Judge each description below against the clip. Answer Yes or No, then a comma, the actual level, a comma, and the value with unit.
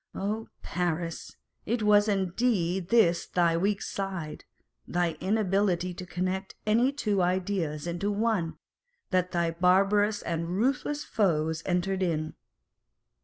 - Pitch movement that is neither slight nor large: Yes, average, 3.2 semitones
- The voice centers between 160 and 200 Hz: Yes, medium, 185 Hz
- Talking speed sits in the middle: No, slow, 120 wpm